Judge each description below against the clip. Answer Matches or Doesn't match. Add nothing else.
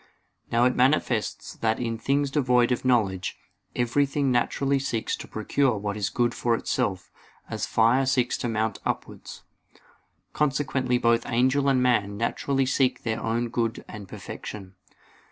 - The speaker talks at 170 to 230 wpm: Doesn't match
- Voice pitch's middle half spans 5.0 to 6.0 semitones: Doesn't match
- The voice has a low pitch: Matches